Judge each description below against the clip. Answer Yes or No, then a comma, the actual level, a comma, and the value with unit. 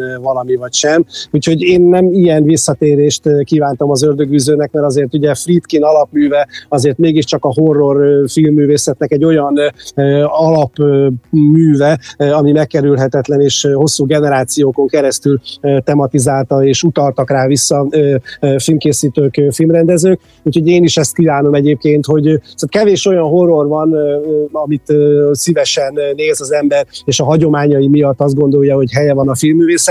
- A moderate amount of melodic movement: No, narrow, 1.8 semitones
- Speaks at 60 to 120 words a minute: No, average, 130 wpm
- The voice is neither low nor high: Yes, medium, 145 Hz